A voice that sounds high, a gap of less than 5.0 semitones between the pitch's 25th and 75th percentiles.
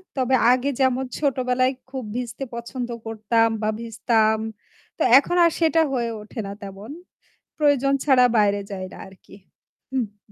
Yes: high, 245 Hz; average, 3.3 semitones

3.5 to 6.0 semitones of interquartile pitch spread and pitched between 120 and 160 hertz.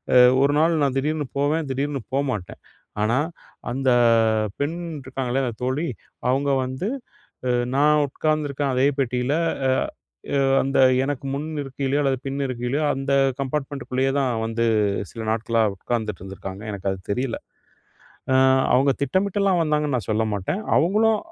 No: average, 3.0 semitones; low, 135 Hz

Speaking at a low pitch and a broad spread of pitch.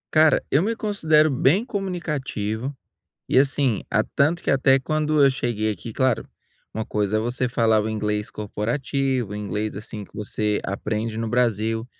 No: low, 120 Hz; average, 4.9 semitones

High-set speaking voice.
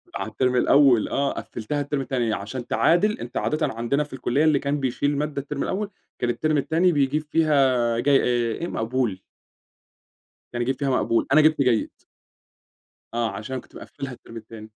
No: low, 135 Hz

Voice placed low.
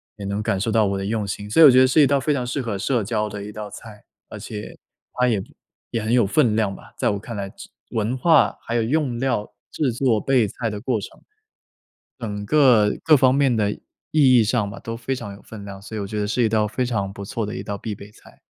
Yes: low, 110 Hz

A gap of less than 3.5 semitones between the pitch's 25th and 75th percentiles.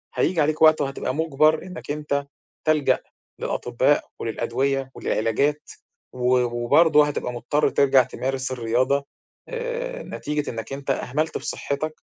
Yes: average, 3.1 semitones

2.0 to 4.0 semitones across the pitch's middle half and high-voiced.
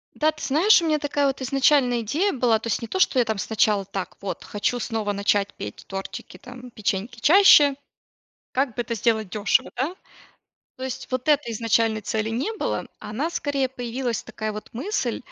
No: average, 4.4 semitones; high, 240 Hz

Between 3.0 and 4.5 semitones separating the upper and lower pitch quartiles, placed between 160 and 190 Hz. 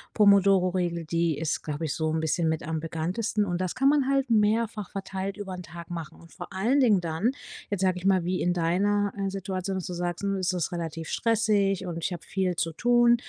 Yes: average, 3.3 semitones; medium, 185 Hz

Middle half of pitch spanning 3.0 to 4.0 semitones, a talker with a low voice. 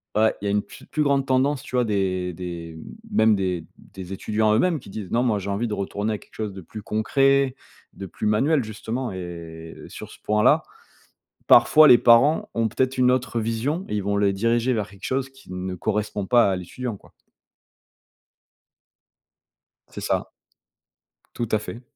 No: average, 4.5 semitones; low, 110 Hz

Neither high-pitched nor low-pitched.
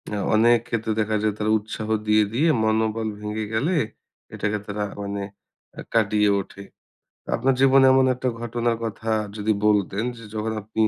No: low, 110 Hz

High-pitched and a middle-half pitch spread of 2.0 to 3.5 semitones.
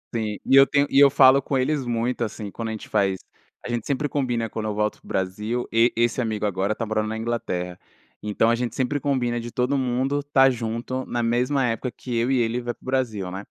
No: low, 120 Hz; average, 3.0 semitones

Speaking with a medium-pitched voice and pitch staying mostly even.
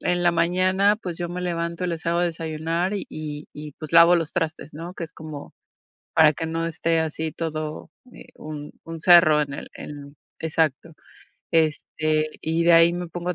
Yes: medium, 165 Hz; narrow, 1.8 semitones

